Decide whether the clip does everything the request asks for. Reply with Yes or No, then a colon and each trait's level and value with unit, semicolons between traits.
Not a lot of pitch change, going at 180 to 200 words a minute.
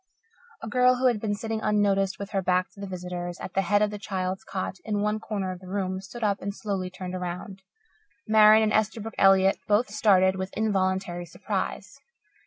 Yes: narrow, 2.2 semitones; average, 195 wpm